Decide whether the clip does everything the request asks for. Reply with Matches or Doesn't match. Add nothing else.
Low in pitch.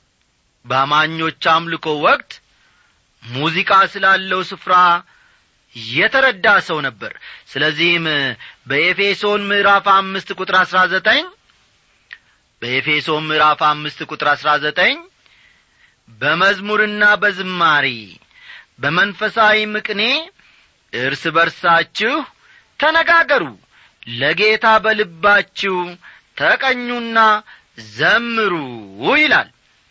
Doesn't match